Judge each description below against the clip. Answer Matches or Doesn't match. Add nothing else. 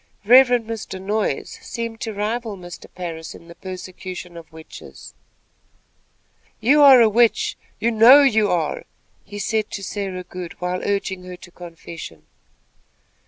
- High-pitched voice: Matches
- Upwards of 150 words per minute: Doesn't match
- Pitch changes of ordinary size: Matches